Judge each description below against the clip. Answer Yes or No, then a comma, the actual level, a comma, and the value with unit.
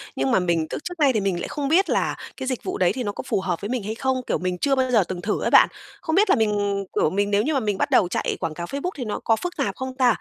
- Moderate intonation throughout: No, wide, 5.8 semitones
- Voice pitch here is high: Yes, high, 220 Hz